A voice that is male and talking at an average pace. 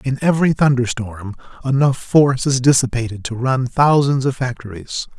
Yes: male; average, 150 wpm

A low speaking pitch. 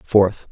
Yes: low, 100 Hz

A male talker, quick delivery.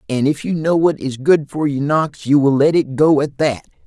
Yes: male; fast, 265 wpm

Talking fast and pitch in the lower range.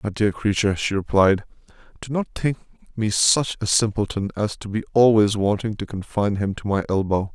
No: average, 190 wpm; low, 105 Hz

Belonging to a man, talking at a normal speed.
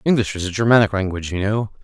No: male; fast, 230 wpm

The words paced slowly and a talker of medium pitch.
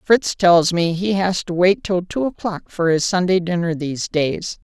No: fast, 205 wpm; medium, 180 Hz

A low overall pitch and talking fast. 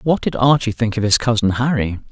Yes: low, 115 Hz; fast, 225 wpm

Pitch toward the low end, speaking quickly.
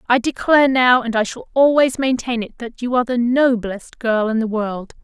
No: high, 240 Hz; fast, 215 wpm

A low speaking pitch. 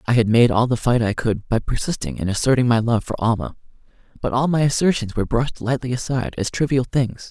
Yes: low, 120 Hz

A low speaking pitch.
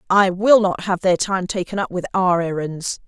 No: medium, 185 Hz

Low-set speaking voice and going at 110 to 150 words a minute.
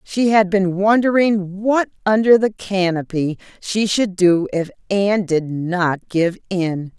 No: high, 190 Hz; average, 145 wpm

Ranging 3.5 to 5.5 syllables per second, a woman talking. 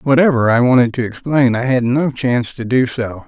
No: 5.3 syllables/s; male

